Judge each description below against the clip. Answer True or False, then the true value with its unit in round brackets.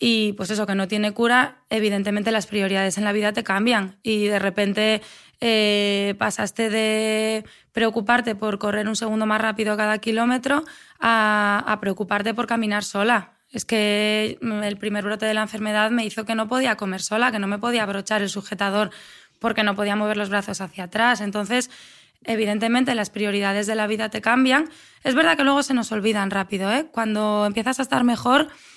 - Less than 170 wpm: False (185 wpm)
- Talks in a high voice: True (215 Hz)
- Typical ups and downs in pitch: False (1.9 semitones)